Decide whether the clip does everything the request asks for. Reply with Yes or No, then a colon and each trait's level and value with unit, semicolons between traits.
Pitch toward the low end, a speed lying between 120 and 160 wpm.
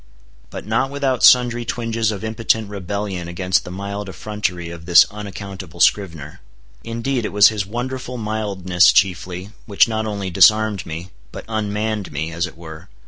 Yes: low, 100 Hz; average, 155 wpm